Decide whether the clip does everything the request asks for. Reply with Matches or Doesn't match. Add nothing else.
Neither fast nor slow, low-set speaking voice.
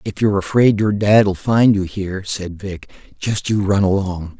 Matches